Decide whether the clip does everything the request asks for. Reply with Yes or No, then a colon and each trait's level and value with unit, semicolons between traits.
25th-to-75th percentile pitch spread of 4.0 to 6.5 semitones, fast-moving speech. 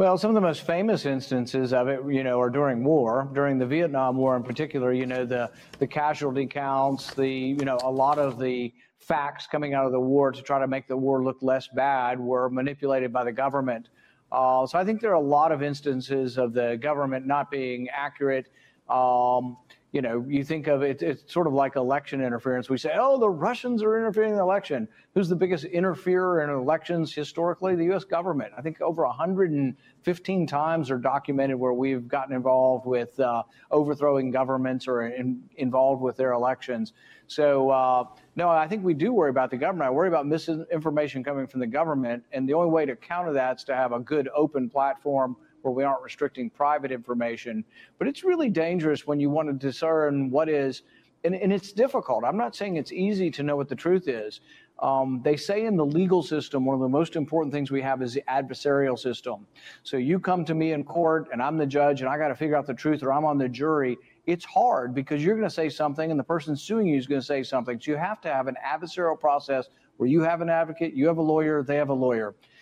No: average, 3.5 semitones; fast, 220 wpm